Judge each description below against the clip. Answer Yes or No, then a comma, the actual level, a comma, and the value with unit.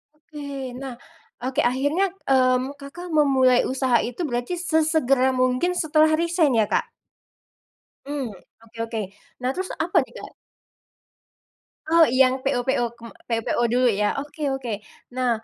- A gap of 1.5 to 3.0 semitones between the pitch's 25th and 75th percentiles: No, average, 3.8 semitones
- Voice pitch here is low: No, very high, 265 Hz